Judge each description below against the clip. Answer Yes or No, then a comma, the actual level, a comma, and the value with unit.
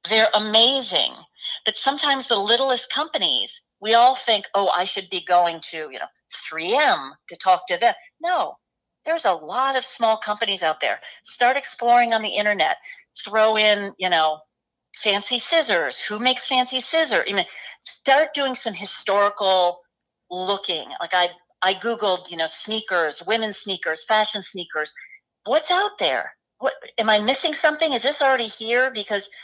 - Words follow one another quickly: No, average, 155 wpm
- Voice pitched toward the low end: No, high, 220 Hz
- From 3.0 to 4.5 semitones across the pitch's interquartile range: No, wide, 5.5 semitones